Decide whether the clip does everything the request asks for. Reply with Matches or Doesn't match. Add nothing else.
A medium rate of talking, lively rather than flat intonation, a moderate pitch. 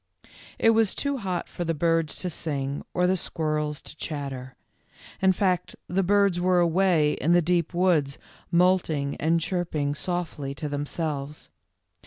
Doesn't match